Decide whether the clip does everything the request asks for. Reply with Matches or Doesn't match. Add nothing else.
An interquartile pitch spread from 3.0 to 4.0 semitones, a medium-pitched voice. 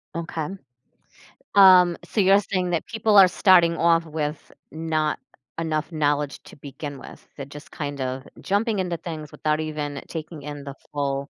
Matches